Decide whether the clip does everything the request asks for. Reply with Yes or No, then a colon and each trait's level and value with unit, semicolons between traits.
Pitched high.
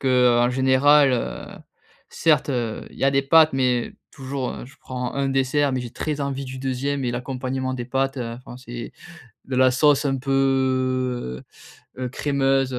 No: low, 130 Hz